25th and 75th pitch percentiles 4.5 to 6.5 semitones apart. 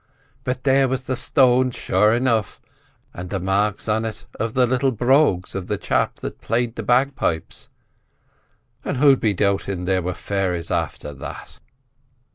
Yes: average, 5.0 semitones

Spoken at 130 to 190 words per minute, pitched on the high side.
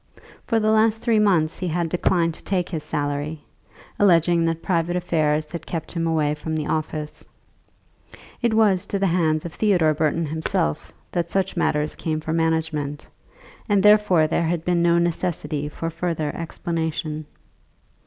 No: average, 160 wpm; medium, 165 Hz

